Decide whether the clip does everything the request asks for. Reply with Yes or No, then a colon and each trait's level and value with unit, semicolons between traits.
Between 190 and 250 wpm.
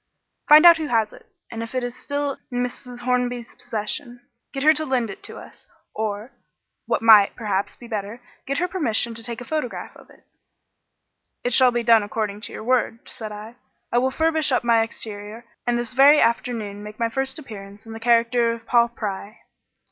Yes: average, 200 wpm